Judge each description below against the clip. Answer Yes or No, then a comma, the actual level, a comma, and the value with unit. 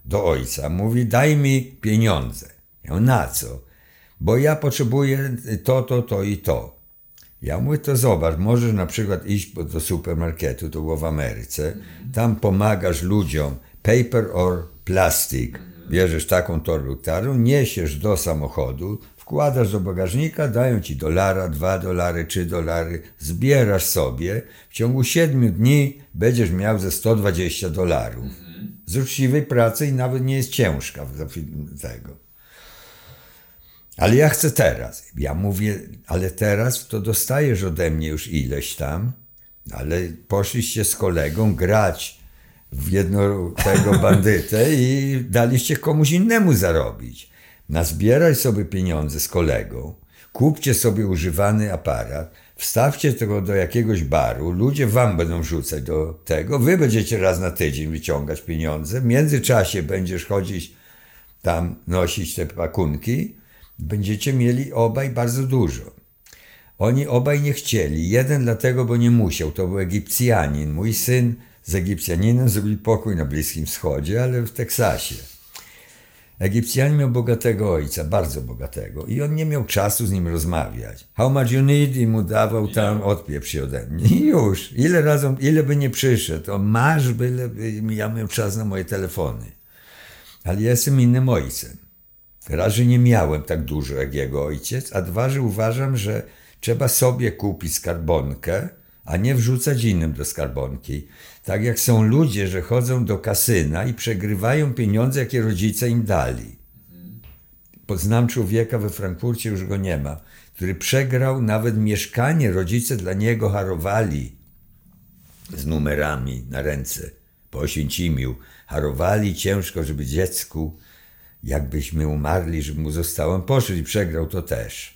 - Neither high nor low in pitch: No, low, 100 Hz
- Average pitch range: No, wide, 6.7 semitones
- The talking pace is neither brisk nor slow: Yes, average, 140 wpm